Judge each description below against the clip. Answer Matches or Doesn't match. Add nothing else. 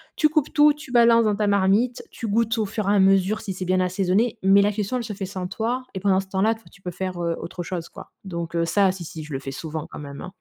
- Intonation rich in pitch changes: Doesn't match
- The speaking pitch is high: Matches